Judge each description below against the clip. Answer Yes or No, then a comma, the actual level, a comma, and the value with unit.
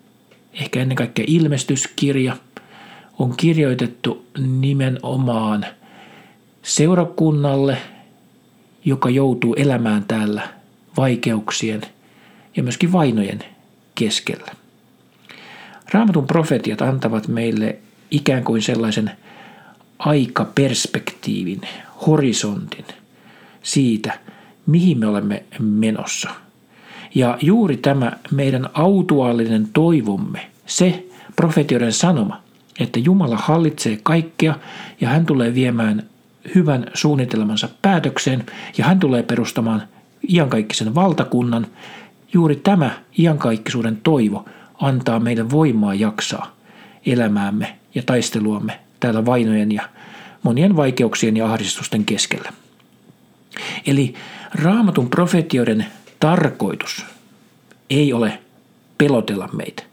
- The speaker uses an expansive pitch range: Yes, wide, 6.7 semitones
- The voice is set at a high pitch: No, low, 135 Hz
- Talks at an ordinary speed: No, slow, 85 wpm